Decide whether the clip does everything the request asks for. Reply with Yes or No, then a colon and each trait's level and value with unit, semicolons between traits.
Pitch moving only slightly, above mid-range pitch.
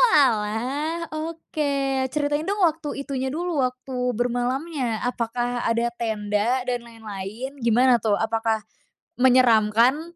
No: average, 4.0 semitones; very high, 250 Hz